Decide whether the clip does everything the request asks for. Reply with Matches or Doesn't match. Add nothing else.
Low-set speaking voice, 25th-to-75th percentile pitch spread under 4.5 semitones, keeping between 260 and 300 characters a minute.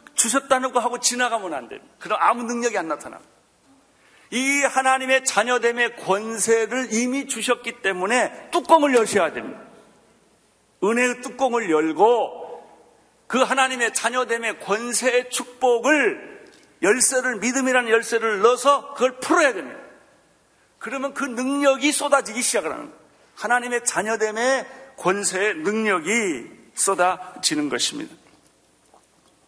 Doesn't match